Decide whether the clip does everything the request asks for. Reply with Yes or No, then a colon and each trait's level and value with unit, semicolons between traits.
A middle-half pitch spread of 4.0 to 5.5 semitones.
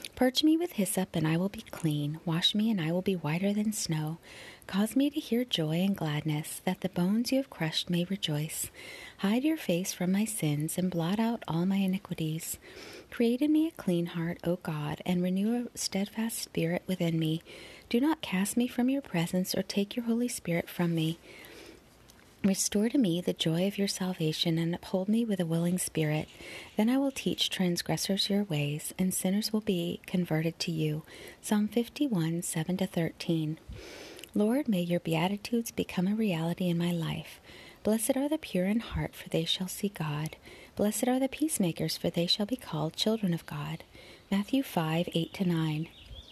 Yes: average, 4.8 semitones